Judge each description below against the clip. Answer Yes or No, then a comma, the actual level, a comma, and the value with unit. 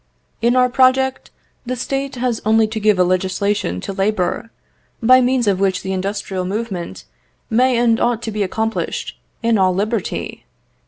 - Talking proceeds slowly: No, average, 160 wpm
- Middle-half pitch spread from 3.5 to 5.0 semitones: Yes, average, 4.0 semitones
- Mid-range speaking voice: No, high, 220 Hz